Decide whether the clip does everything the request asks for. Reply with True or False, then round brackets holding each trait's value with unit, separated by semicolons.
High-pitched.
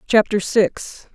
True (205 Hz)